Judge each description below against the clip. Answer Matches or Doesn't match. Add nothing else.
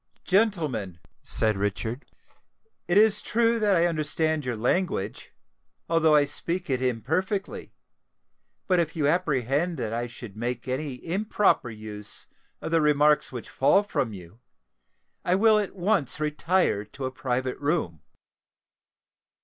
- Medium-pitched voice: Matches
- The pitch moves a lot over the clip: Matches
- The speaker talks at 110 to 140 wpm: Matches